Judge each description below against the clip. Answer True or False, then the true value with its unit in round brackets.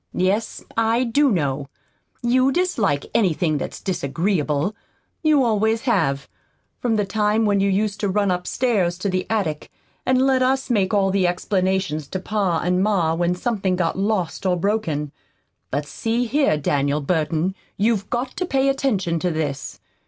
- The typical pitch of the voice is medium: False (195 Hz)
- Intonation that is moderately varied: True (5.0 semitones)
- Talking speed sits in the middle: True (160 wpm)